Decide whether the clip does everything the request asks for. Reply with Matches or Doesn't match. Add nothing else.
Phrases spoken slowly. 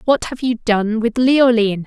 Doesn't match